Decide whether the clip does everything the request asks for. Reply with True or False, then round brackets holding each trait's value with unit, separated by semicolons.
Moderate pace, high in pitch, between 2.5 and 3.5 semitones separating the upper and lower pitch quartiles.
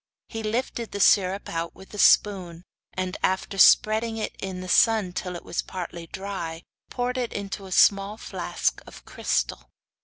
True (165 wpm; 195 Hz; 2.9 semitones)